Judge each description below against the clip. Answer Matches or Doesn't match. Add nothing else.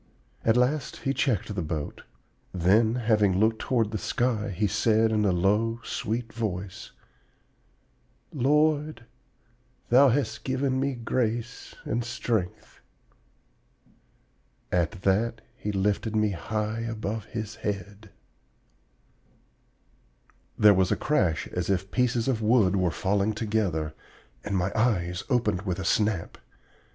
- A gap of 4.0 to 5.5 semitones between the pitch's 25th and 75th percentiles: Doesn't match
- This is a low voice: Matches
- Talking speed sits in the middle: Doesn't match